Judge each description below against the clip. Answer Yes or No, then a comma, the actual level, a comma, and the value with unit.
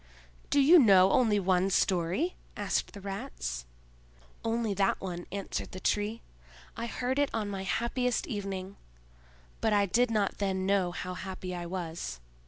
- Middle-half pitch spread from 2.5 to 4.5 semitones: Yes, average, 3.6 semitones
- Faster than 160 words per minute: No, average, 155 wpm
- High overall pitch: Yes, high, 195 Hz